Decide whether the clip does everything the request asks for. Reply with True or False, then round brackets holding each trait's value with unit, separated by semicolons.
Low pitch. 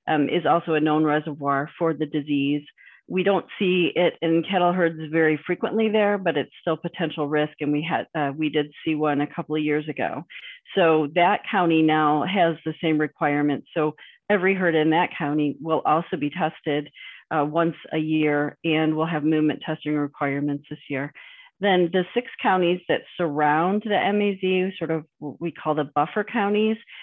False (155 Hz)